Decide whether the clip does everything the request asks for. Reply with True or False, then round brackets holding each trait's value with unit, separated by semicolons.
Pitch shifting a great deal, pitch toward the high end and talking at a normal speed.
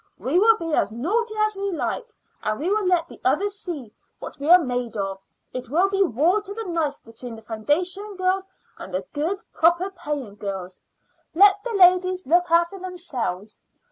True (7.8 semitones; 340 Hz; 185 wpm)